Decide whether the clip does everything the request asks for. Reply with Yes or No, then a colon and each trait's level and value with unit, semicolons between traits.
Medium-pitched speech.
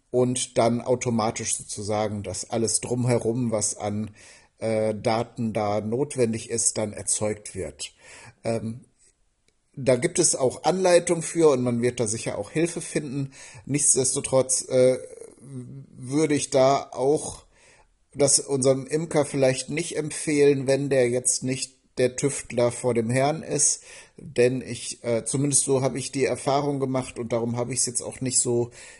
No: low, 130 Hz